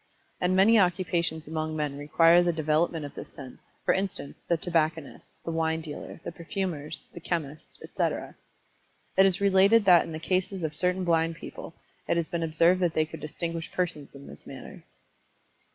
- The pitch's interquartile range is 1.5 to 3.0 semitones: Yes, narrow, 2.5 semitones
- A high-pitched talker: No, medium, 165 Hz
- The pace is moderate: Yes, average, 175 wpm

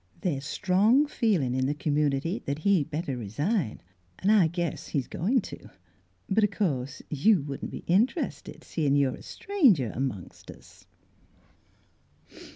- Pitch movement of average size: No, wide, 6.6 semitones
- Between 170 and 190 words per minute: No, average, 145 wpm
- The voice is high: No, medium, 160 Hz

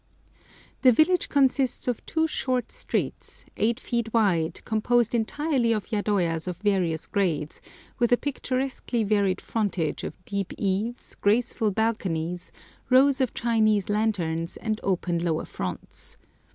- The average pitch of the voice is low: No, high, 215 Hz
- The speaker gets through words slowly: Yes, slow, 125 wpm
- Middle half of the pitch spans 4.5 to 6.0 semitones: Yes, average, 4.9 semitones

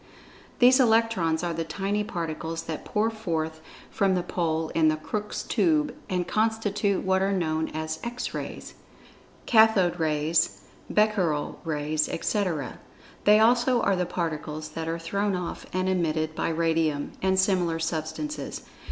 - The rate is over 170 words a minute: No, average, 145 wpm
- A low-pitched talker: No, medium, 175 Hz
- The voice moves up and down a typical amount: Yes, average, 4.7 semitones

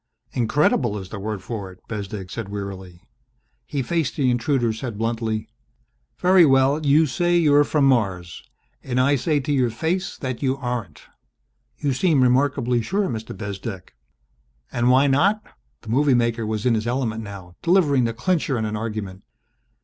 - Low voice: Yes, low, 120 Hz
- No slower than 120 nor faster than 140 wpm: No, average, 165 wpm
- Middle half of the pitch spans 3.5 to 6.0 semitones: Yes, average, 4.8 semitones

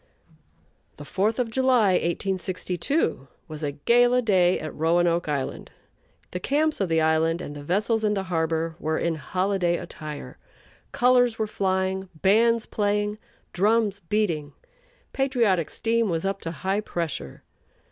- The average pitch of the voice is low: No, high, 190 Hz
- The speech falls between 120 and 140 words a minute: Yes, slow, 135 wpm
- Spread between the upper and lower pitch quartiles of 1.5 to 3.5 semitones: No, average, 4.9 semitones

